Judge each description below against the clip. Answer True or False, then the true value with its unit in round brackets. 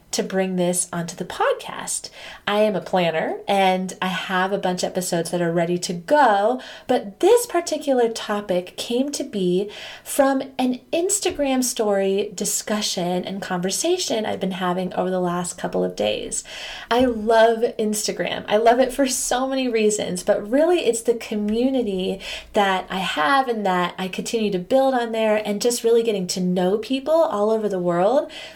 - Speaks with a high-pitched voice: True (210 Hz)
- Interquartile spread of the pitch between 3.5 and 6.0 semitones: True (5.1 semitones)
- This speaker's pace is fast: False (170 wpm)